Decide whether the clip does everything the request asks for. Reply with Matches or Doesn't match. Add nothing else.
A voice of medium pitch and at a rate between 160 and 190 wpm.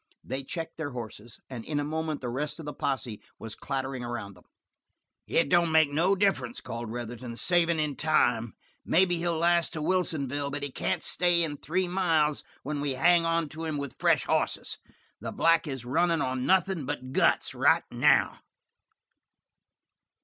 Matches